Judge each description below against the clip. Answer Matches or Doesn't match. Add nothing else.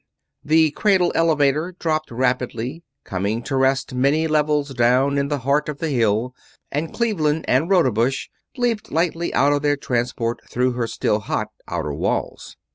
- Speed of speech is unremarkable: Matches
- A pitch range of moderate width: Matches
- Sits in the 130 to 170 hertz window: Matches